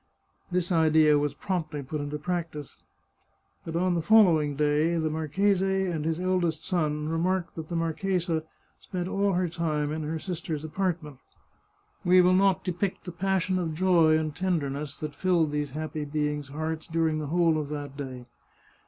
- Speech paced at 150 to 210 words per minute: Yes, average, 175 wpm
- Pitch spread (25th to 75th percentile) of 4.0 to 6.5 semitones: No, average, 3.0 semitones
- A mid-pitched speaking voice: Yes, medium, 160 Hz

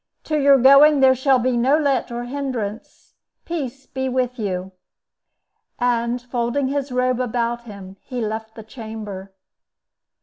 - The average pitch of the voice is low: No, high, 245 Hz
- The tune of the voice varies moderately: Yes, average, 3.1 semitones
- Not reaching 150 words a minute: Yes, average, 140 wpm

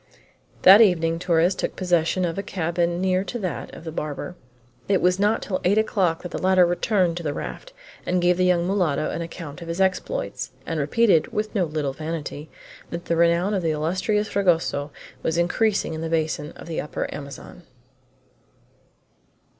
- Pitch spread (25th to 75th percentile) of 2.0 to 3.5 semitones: Yes, average, 2.7 semitones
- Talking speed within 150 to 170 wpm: No, average, 180 wpm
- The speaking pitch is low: No, medium, 175 Hz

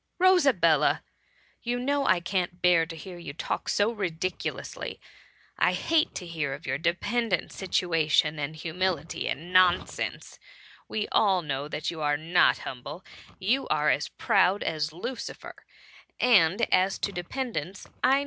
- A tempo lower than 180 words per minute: Yes, average, 155 wpm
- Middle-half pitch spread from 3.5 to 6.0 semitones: Yes, average, 4.4 semitones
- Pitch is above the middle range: No, medium, 175 Hz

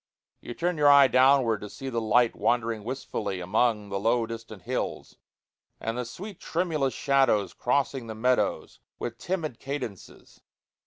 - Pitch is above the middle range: No, low, 120 Hz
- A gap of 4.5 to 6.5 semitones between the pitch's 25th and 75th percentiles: No, average, 3.7 semitones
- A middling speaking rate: Yes, average, 150 wpm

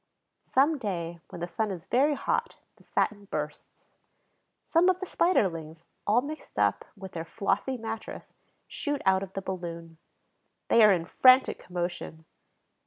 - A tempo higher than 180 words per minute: No, average, 150 wpm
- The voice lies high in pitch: Yes, high, 195 Hz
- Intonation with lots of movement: Yes, wide, 7.1 semitones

